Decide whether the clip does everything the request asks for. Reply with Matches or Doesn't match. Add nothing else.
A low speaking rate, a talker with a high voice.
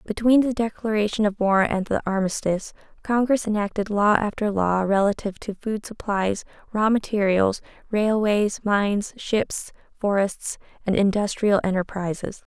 Matches